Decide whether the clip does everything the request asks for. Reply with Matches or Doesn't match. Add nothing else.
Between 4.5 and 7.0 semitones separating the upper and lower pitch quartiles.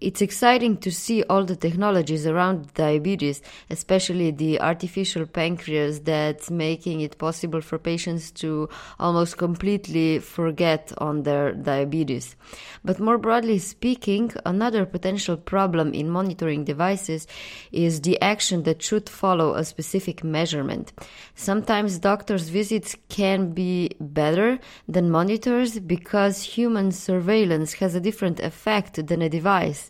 Doesn't match